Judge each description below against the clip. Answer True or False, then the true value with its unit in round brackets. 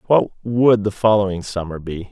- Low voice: True (100 Hz)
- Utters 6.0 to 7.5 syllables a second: False (5.0 syllables/s)